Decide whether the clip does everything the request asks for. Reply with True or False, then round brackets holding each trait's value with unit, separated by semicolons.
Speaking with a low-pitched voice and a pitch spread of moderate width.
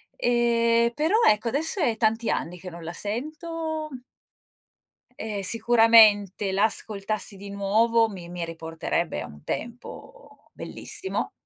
False (220 Hz; 3.3 semitones)